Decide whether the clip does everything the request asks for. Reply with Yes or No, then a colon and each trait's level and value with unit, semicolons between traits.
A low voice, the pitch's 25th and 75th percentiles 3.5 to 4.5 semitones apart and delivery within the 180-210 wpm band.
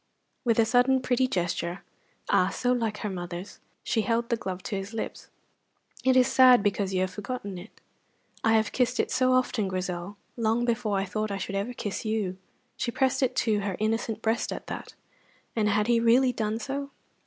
No: high, 220 Hz; average, 3.8 semitones; average, 195 wpm